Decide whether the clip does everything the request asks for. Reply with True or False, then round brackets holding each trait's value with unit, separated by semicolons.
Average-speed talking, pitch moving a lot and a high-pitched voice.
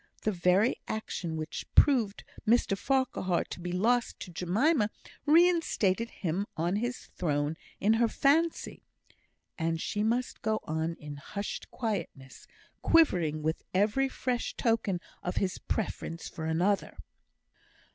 False (125 wpm; 6.2 semitones; 200 Hz)